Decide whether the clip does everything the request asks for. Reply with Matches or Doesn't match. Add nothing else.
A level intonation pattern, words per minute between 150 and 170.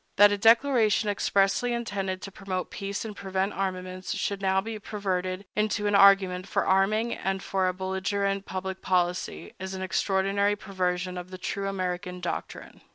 Matches